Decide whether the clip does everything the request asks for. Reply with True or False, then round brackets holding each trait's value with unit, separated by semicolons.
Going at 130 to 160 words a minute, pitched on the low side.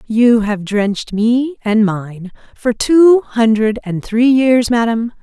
False (150 wpm; 230 Hz)